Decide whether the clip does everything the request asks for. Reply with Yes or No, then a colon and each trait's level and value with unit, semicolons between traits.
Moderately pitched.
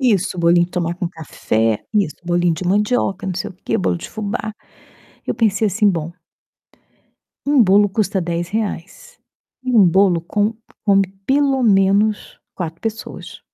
No: high, 195 Hz